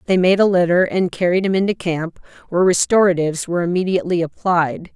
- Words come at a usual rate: Yes, average, 170 wpm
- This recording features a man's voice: No, female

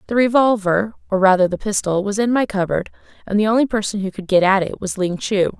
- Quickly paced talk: Yes, fast, 235 wpm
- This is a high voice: Yes, high, 205 Hz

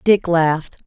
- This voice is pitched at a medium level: Yes, medium, 170 Hz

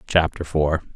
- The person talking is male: Yes, male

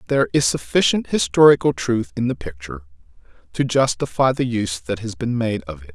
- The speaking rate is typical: Yes, average, 180 wpm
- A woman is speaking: No, male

